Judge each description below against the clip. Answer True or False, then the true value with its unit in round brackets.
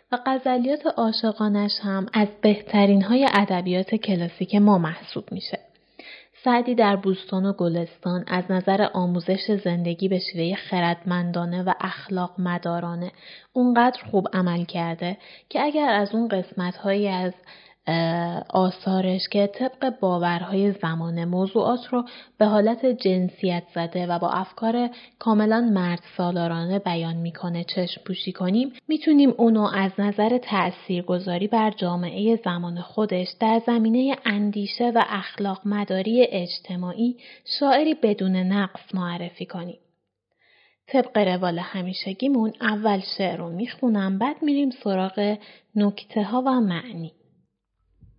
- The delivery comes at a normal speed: True (120 wpm)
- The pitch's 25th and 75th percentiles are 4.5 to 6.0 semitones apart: False (3.9 semitones)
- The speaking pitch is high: True (195 Hz)